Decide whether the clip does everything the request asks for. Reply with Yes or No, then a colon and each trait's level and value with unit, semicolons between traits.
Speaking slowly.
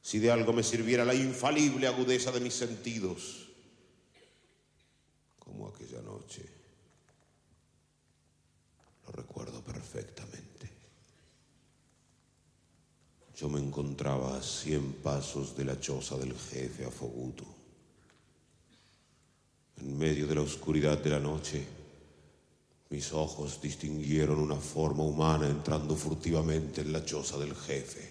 Yes: slow, 105 wpm